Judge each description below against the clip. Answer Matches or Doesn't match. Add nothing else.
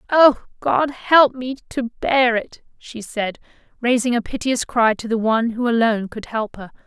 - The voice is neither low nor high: Doesn't match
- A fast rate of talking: Doesn't match